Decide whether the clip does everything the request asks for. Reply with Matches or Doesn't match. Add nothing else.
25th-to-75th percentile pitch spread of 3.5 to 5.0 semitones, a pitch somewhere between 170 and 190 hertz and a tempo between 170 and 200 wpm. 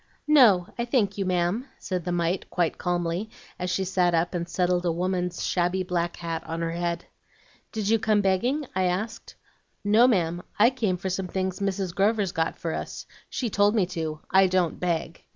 Doesn't match